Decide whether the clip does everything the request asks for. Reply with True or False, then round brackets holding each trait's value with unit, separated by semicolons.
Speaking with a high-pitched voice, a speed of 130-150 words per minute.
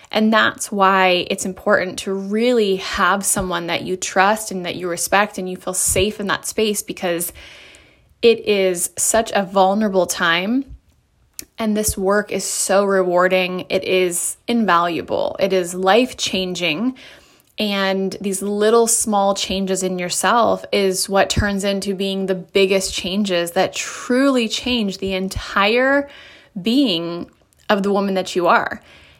True (195 Hz; 145 wpm)